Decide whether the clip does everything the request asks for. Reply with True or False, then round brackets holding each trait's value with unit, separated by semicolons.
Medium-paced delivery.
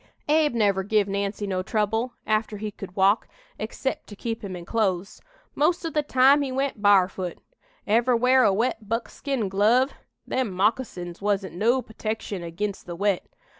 True (165 wpm)